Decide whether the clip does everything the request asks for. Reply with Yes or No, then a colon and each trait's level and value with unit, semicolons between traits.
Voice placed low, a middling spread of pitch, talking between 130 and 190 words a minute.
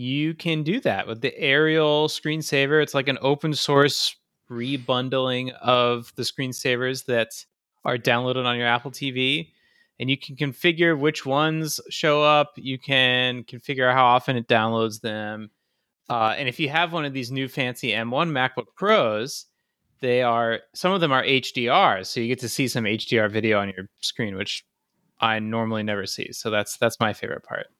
Yes: low, 130 Hz; average, 3.9 semitones; average, 175 wpm